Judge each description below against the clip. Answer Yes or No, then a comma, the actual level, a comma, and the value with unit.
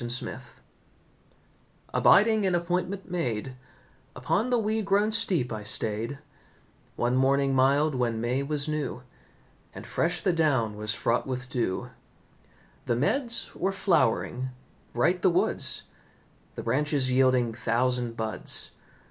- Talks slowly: Yes, slow, 125 wpm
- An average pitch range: No, wide, 6.7 semitones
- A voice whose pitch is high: No, low, 135 Hz